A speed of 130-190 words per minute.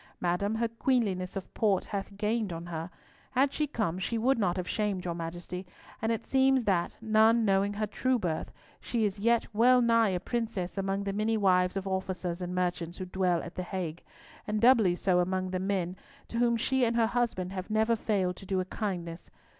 No: fast, 205 wpm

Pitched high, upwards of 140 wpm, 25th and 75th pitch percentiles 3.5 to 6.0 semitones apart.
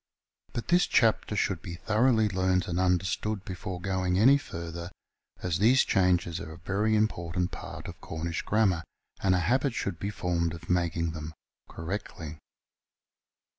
No: very low, 90 Hz; average, 150 wpm; average, 3.8 semitones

